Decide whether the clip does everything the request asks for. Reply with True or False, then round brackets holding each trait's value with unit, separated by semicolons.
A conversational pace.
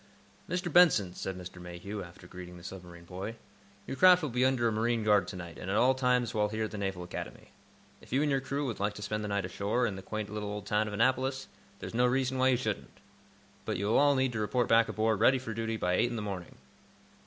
False (255 wpm)